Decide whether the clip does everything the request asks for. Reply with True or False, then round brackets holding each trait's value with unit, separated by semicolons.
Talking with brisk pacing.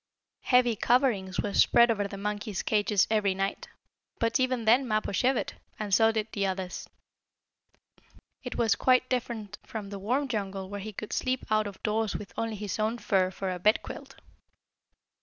False (170 wpm)